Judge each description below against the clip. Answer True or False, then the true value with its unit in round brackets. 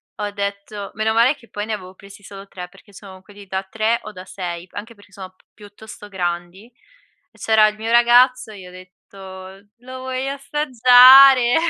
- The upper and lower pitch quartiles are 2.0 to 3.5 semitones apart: False (3.9 semitones)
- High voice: True (205 Hz)